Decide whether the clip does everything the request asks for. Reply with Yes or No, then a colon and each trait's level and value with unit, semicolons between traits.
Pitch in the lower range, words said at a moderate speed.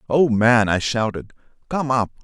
Yes: low, 120 Hz; average, 160 wpm